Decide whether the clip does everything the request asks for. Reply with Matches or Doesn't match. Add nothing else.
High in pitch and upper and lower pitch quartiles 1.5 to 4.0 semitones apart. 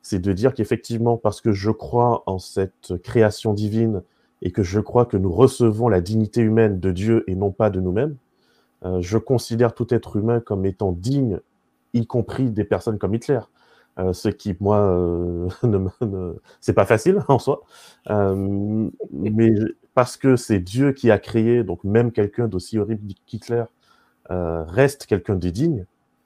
Doesn't match